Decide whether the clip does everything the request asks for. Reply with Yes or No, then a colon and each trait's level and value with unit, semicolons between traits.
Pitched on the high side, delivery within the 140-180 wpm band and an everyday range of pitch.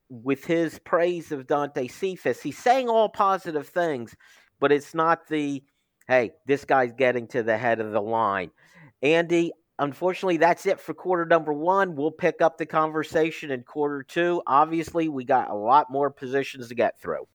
No: medium, 155 Hz; average, 175 wpm; average, 3.9 semitones